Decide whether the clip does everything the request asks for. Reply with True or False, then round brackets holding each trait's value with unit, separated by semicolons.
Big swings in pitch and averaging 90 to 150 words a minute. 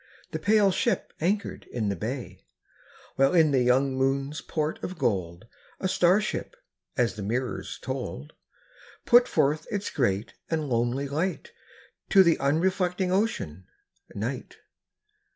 True (7.4 semitones; 140 wpm)